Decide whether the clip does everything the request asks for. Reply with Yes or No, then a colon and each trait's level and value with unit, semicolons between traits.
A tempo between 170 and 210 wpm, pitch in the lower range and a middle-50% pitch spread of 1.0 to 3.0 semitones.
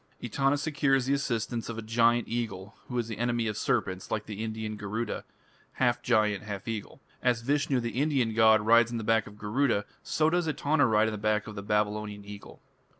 Yes: fast, 205 wpm; low, 115 Hz; narrow, 2.6 semitones